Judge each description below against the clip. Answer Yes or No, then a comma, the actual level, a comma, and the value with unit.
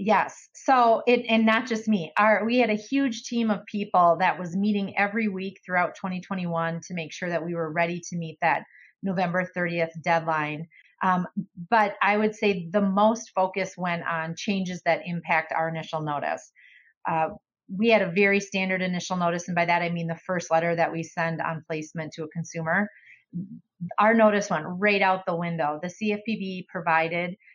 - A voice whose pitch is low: No, medium, 185 Hz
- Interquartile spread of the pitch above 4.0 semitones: No, average, 3.6 semitones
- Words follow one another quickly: No, average, 185 wpm